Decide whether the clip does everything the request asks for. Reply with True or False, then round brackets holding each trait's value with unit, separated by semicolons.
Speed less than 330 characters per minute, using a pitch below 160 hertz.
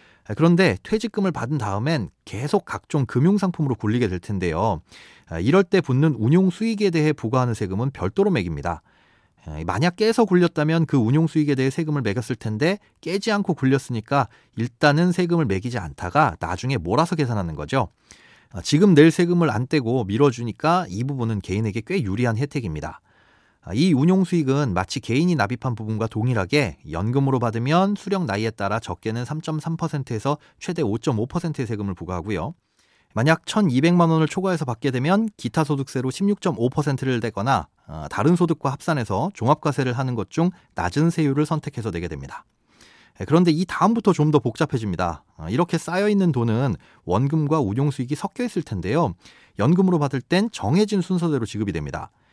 False (355 characters per minute; 140 Hz)